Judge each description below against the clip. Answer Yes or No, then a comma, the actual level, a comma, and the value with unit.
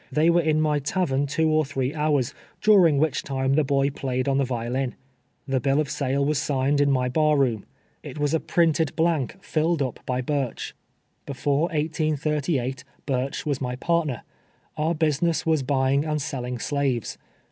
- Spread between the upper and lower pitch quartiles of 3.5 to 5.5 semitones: No, average, 2.7 semitones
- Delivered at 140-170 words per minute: No, average, 180 wpm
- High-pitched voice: No, medium, 145 Hz